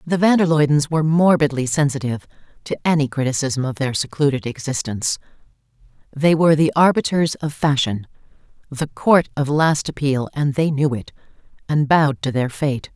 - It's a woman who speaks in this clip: Yes, female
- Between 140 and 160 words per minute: Yes, average, 155 wpm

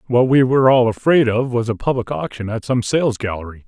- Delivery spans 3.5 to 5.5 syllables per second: No, 5.7 syllables/s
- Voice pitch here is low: Yes, low, 120 Hz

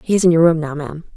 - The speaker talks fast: Yes, fast, 360 wpm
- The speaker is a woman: Yes, female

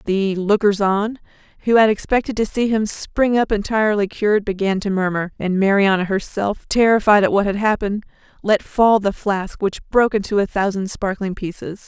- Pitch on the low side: No, high, 205 Hz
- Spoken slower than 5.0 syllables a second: No, 5.2 syllables/s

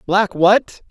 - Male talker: Yes, male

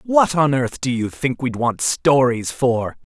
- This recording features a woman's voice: No, male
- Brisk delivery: No, average, 190 wpm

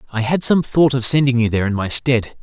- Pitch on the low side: Yes, low, 125 Hz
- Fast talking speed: Yes, fast, 270 wpm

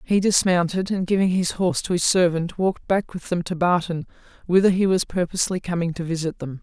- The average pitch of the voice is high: No, medium, 175 Hz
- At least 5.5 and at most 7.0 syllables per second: Yes, 5.9 syllables/s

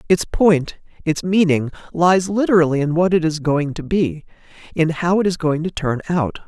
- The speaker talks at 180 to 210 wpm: Yes, average, 195 wpm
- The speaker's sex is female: No, male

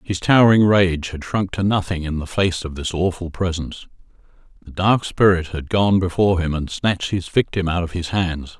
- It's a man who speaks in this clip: Yes, male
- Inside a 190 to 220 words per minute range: Yes, average, 200 wpm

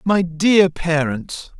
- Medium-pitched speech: Yes, medium, 170 Hz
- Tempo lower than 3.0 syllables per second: Yes, 2.8 syllables/s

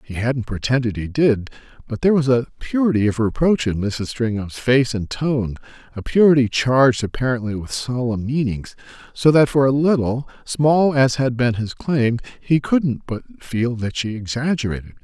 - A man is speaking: Yes, male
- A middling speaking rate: Yes, average, 170 wpm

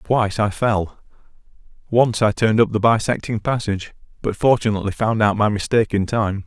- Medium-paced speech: Yes, average, 165 wpm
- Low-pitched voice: Yes, low, 110 Hz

